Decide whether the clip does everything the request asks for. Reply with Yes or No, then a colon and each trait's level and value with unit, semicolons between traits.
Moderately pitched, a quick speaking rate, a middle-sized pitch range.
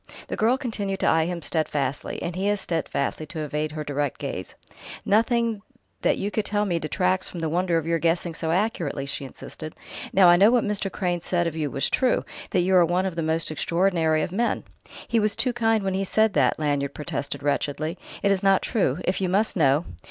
Yes: medium, 175 Hz; fast, 215 wpm; average, 4.3 semitones